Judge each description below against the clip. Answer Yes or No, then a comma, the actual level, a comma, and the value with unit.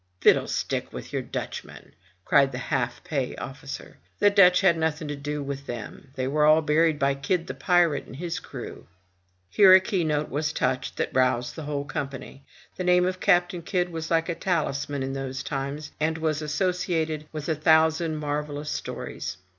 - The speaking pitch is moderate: Yes, medium, 150 Hz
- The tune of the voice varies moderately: Yes, average, 3.3 semitones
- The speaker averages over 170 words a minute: Yes, average, 185 wpm